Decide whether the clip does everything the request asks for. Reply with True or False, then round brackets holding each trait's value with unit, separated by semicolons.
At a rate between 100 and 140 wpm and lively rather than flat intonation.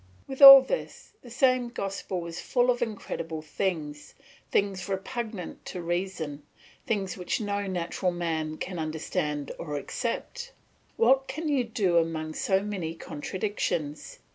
True (135 wpm; 6.1 semitones)